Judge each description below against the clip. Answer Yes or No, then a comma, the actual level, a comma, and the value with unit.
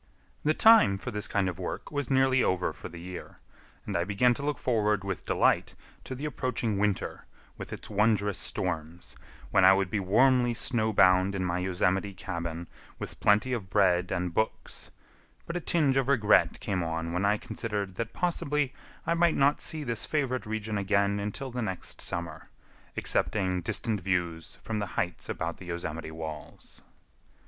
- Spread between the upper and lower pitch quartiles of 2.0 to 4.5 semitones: No, average, 5.3 semitones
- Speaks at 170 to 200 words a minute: Yes, average, 175 wpm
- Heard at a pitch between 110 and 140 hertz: No, low, 100 Hz